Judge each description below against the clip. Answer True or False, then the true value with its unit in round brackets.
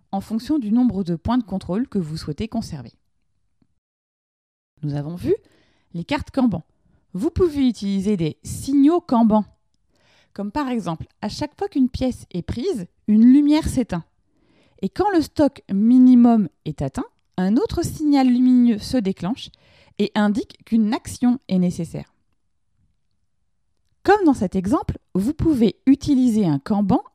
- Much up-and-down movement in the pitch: True (6.4 semitones)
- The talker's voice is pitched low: False (225 Hz)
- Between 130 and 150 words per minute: True (145 wpm)